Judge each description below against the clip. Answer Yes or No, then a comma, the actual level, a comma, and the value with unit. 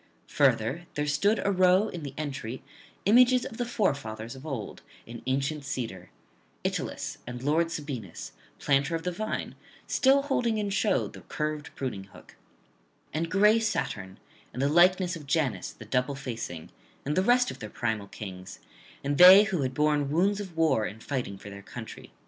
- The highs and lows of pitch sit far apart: Yes, wide, 7.2 semitones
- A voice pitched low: No, medium, 150 Hz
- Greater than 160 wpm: Yes, average, 170 wpm